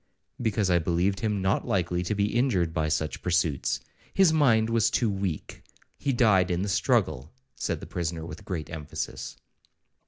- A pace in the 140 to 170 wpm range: Yes, average, 160 wpm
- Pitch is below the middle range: Yes, very low, 95 Hz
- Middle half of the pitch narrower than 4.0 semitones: No, average, 4.7 semitones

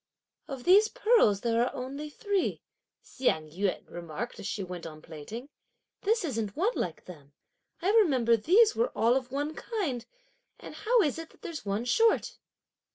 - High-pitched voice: Yes, very high, 255 Hz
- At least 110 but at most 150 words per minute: No, average, 165 wpm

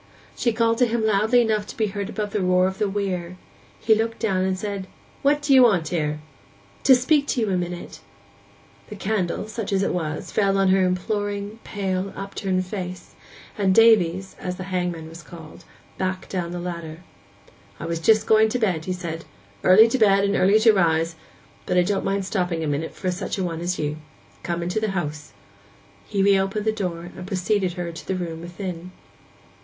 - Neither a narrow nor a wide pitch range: Yes, average, 3.1 semitones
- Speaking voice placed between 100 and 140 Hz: No, high, 190 Hz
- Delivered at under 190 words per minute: No, average, 195 wpm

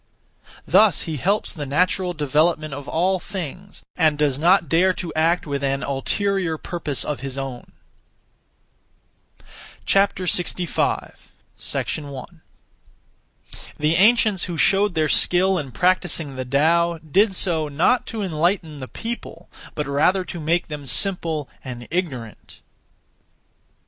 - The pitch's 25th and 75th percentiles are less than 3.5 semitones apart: No, average, 4.2 semitones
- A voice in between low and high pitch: Yes, medium, 165 Hz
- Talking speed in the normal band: No, slow, 125 wpm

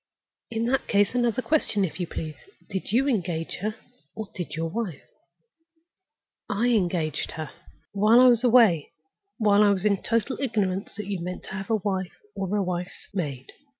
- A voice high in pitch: Yes, high, 200 Hz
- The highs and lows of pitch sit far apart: No, average, 4.1 semitones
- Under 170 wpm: No, average, 175 wpm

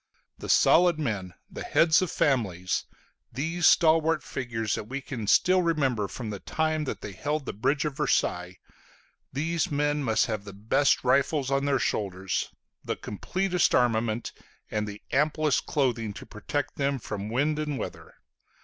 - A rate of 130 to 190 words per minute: Yes, average, 160 wpm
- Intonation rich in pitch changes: Yes, wide, 5.9 semitones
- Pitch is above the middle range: No, low, 135 Hz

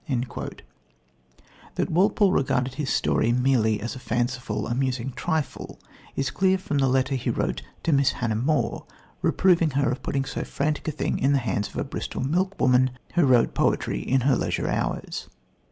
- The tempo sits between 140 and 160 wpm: No, average, 170 wpm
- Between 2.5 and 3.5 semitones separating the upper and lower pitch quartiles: Yes, average, 3.2 semitones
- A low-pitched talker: Yes, low, 130 Hz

